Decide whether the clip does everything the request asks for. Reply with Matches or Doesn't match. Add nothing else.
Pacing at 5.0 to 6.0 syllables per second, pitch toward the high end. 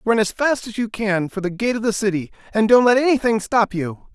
Matches